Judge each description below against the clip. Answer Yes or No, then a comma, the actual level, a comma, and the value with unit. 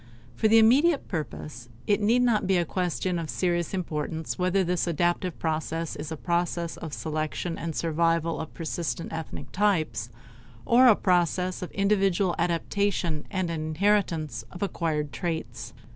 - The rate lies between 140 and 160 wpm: Yes, average, 150 wpm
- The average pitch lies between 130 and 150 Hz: No, medium, 170 Hz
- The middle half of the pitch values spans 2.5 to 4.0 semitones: Yes, average, 3.2 semitones